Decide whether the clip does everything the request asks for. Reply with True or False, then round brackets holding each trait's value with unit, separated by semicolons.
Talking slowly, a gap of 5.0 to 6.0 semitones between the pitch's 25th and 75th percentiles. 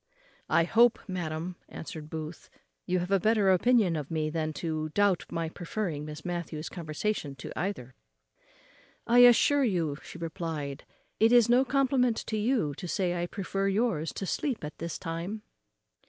False (160 wpm; 5.4 semitones)